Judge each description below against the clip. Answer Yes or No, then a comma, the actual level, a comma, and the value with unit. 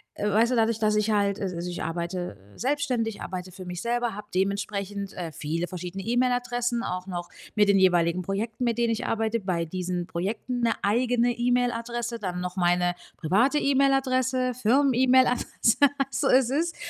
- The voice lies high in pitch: Yes, high, 220 Hz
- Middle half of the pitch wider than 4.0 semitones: Yes, average, 5.1 semitones